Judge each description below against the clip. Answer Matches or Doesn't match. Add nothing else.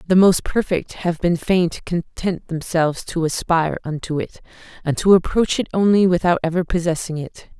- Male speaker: Doesn't match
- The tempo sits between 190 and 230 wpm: Doesn't match